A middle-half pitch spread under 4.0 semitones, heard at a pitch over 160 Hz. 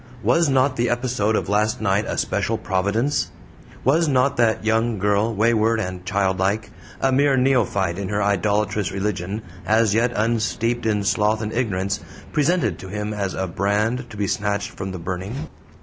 No: average, 2.9 semitones; low, 105 Hz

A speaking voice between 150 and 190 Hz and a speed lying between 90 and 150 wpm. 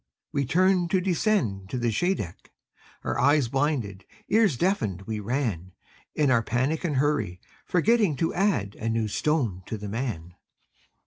No: low, 130 Hz; average, 145 wpm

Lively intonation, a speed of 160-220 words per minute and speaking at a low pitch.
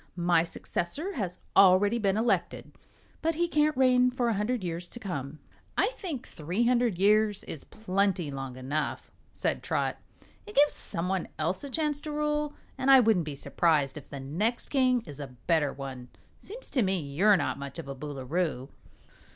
No: wide, 8.8 semitones; average, 180 wpm; high, 195 Hz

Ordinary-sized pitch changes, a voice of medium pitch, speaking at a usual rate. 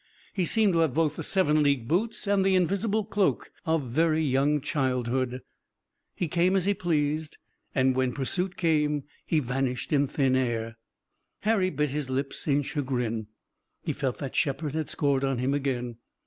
Yes: average, 4.4 semitones; medium, 145 Hz; average, 170 wpm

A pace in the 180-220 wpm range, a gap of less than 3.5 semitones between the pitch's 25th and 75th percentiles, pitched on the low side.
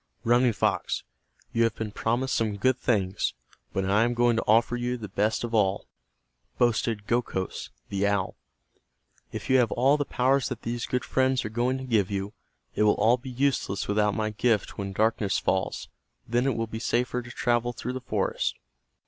Yes: average, 190 wpm; average, 2.8 semitones; low, 115 Hz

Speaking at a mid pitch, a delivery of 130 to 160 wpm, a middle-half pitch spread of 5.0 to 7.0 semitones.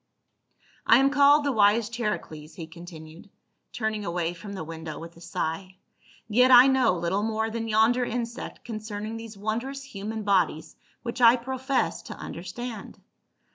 No: high, 215 Hz; average, 150 wpm; wide, 5.4 semitones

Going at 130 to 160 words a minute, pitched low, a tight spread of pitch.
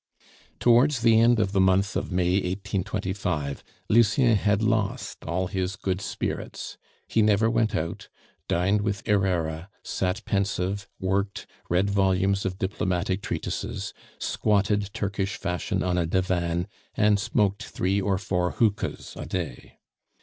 Yes: slow, 135 wpm; low, 100 Hz; narrow, 2.2 semitones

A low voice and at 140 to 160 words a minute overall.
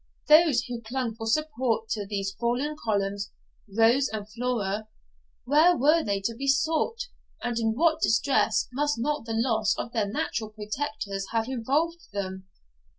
No: high, 230 Hz; average, 150 wpm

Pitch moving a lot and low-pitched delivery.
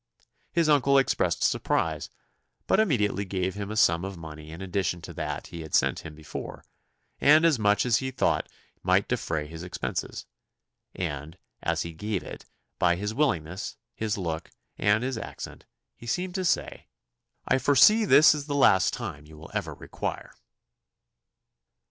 Yes: wide, 8.5 semitones; low, 100 Hz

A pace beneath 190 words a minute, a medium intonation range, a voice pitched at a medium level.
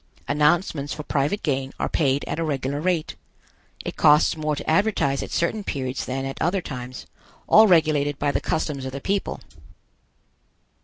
Yes: average, 165 wpm; average, 3.2 semitones; medium, 150 Hz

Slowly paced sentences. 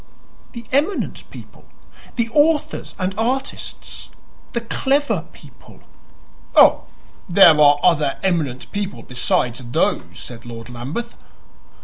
Yes: slow, 105 wpm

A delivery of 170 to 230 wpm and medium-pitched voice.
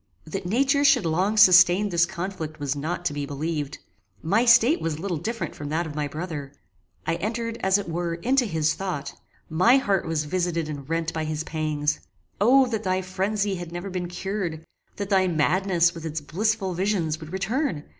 Yes: average, 185 wpm; medium, 175 Hz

